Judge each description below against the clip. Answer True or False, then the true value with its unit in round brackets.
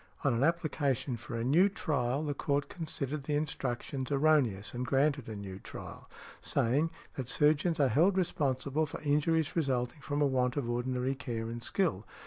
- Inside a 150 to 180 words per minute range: True (170 wpm)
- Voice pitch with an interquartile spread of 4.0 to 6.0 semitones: False (3.6 semitones)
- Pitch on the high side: False (140 Hz)